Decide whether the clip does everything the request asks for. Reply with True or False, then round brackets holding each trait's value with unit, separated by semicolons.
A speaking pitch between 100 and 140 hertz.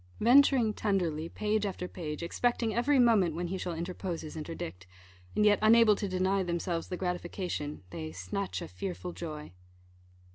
False (180 Hz)